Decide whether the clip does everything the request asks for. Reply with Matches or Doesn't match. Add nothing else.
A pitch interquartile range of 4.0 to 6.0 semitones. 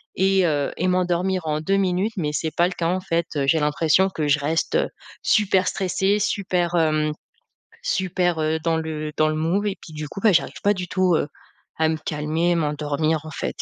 Doesn't match